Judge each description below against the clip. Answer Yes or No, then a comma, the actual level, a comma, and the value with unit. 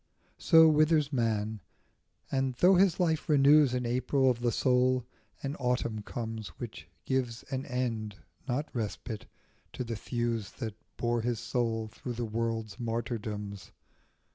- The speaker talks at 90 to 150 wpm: Yes, average, 140 wpm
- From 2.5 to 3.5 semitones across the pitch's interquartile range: Yes, average, 2.9 semitones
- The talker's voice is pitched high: No, low, 120 Hz